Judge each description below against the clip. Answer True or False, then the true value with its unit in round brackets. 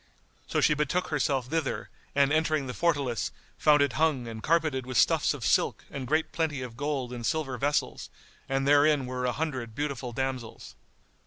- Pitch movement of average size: True (3.1 semitones)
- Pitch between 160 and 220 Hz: False (140 Hz)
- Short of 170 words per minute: False (175 wpm)